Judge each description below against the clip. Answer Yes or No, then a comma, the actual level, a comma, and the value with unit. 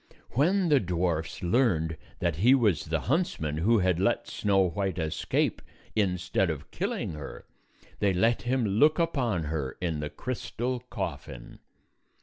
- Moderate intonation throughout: No, wide, 7.0 semitones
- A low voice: Yes, very low, 95 Hz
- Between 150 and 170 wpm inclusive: No, average, 140 wpm